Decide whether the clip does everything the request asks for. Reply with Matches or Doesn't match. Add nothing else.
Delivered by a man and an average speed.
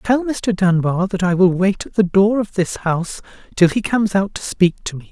Doesn't match